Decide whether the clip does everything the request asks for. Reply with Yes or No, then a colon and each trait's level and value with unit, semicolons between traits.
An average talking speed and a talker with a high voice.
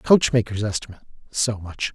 No: average, 155 wpm; low, 110 Hz